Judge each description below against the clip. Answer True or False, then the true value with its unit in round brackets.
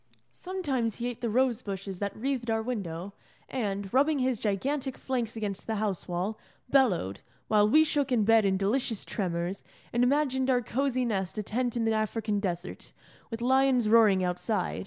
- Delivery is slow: False (175 wpm)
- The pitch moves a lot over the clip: False (4.3 semitones)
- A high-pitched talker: True (225 Hz)